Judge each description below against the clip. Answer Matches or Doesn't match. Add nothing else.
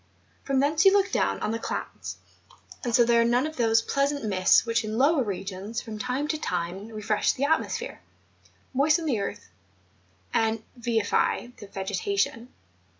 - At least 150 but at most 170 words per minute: Doesn't match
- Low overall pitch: Doesn't match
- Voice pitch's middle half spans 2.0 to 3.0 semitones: Doesn't match